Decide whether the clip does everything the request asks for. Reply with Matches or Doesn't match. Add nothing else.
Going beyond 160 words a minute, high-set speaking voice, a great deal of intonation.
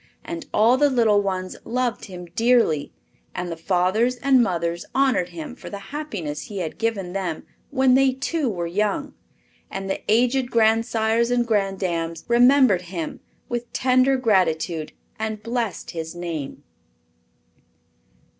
Doesn't match